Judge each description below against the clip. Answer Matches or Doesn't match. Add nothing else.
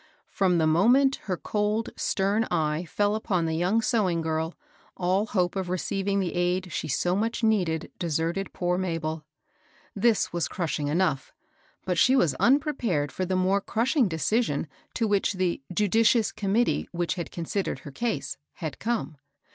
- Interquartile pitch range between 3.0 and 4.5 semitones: Matches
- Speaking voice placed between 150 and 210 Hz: Matches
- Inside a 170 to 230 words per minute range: Doesn't match